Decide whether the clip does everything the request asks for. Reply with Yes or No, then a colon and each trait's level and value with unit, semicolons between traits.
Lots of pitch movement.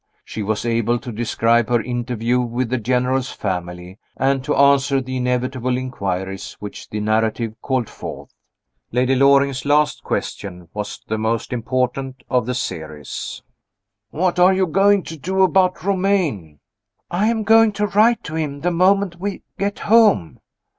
Yes: wide, 7.5 semitones